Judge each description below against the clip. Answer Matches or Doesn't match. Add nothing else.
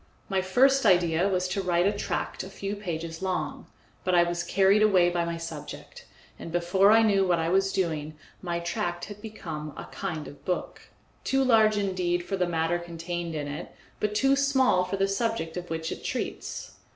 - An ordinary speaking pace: Matches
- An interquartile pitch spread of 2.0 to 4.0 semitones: Matches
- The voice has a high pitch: Doesn't match